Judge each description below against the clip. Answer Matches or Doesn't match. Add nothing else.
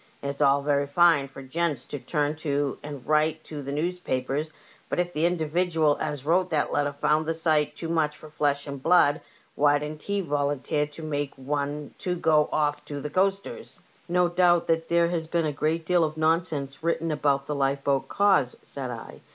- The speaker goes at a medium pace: Matches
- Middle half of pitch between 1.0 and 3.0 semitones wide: Matches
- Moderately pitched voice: Matches